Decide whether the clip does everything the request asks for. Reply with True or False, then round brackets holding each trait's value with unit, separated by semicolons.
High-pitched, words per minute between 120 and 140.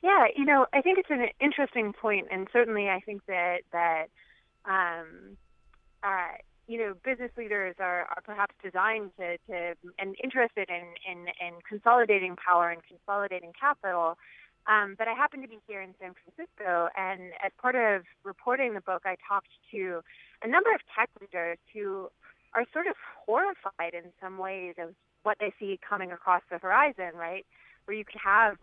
False (195 Hz; 175 wpm)